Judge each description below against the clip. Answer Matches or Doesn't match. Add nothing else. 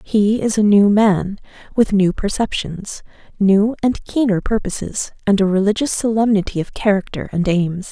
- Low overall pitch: Doesn't match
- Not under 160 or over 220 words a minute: Doesn't match